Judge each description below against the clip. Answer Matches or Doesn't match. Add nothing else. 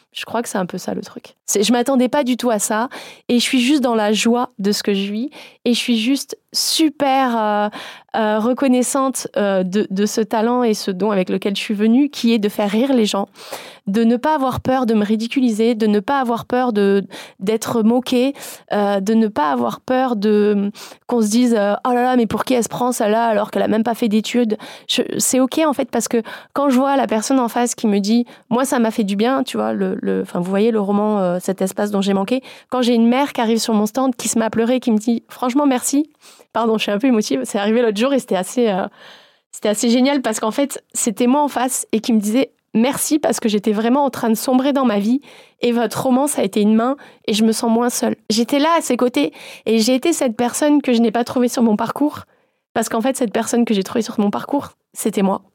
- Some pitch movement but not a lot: Matches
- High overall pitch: Matches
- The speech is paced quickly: Matches